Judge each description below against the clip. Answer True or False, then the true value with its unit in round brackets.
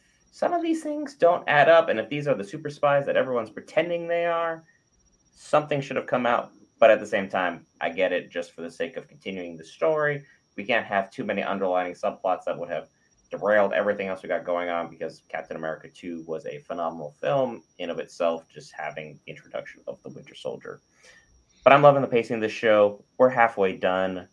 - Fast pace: True (215 wpm)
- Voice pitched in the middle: False (105 Hz)